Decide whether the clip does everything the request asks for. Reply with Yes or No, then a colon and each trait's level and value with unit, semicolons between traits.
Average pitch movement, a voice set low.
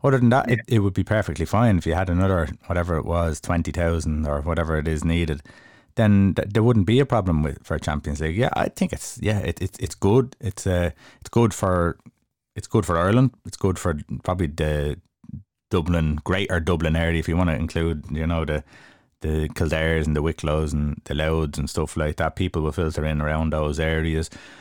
Yes: average, 3.9 semitones; very low, 85 Hz